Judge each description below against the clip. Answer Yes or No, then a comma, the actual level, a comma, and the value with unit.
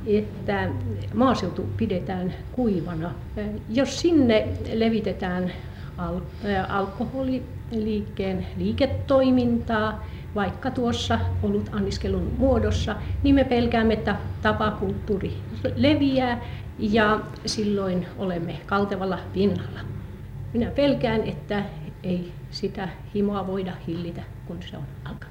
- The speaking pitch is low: No, high, 195 Hz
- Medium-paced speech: No, slow, 90 wpm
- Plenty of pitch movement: Yes, wide, 5.8 semitones